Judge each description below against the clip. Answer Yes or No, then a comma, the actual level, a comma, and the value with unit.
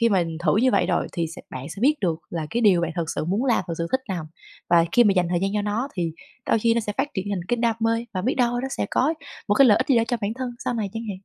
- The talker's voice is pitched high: Yes, high, 210 Hz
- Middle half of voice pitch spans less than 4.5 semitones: No, average, 5.3 semitones